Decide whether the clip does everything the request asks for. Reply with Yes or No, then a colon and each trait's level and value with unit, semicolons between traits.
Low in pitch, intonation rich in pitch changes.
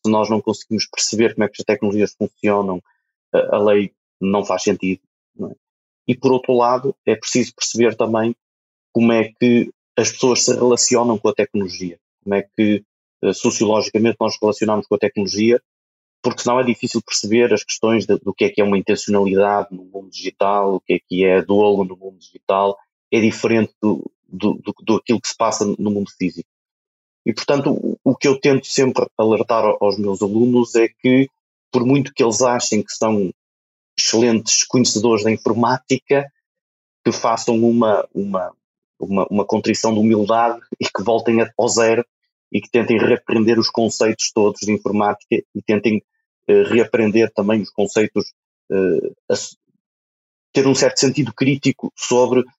No: low, 110 Hz; average, 3.1 semitones